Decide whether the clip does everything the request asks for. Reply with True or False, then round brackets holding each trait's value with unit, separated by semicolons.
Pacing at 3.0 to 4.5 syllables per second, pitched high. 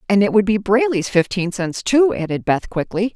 False (5.1 syllables/s; 205 Hz)